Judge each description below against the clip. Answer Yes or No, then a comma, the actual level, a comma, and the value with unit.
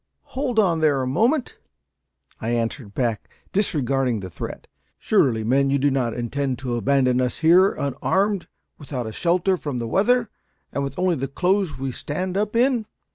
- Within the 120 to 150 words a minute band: No, average, 170 wpm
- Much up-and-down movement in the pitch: Yes, wide, 6.8 semitones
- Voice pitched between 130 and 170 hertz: Yes, medium, 140 Hz